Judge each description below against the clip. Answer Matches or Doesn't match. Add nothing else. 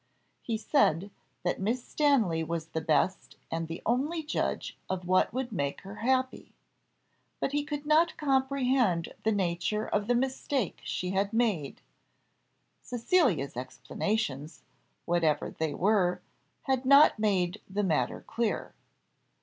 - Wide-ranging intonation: Matches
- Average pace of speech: Doesn't match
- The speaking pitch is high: Matches